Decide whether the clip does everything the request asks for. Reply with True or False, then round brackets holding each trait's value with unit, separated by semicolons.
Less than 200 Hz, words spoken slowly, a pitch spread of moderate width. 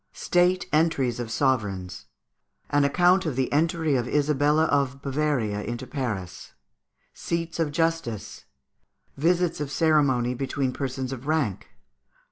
True (140 Hz; 120 wpm; 4.4 semitones)